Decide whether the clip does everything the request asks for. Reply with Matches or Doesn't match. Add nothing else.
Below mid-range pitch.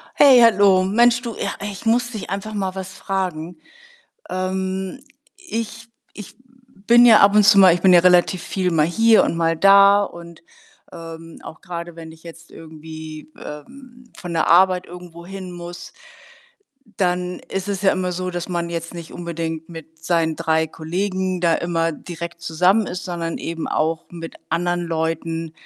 Doesn't match